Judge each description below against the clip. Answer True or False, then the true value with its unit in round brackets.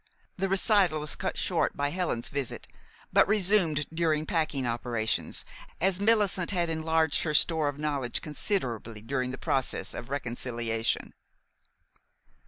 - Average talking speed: False (130 wpm)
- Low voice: False (150 Hz)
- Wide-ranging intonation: True (5.7 semitones)